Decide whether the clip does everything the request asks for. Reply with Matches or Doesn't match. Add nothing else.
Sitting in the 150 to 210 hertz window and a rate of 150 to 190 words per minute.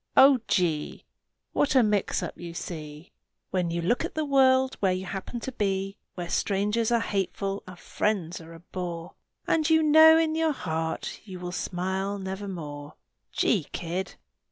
Matches